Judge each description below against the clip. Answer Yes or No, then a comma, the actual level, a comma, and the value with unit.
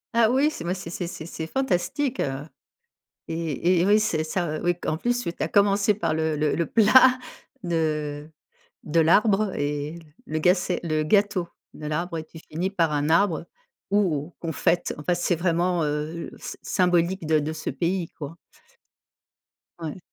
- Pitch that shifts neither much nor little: Yes, average, 3.5 semitones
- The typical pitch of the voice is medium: Yes, medium, 170 Hz